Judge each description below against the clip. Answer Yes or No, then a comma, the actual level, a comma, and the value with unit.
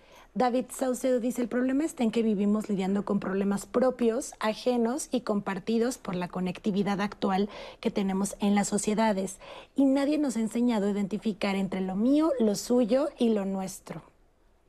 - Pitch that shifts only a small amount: No, average, 3.8 semitones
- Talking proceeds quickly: No, average, 165 wpm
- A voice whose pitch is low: No, high, 220 Hz